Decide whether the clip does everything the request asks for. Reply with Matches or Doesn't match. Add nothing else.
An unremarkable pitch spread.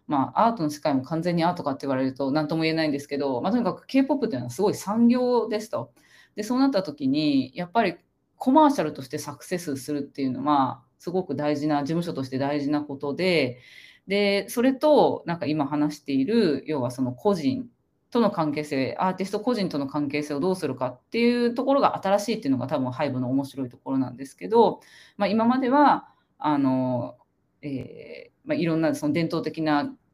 Doesn't match